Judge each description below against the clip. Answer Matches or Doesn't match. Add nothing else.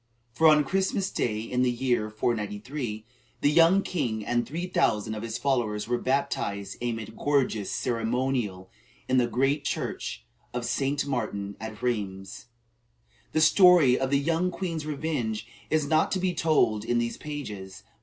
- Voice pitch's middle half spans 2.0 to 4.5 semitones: Doesn't match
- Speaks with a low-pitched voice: Matches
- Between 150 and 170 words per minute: Matches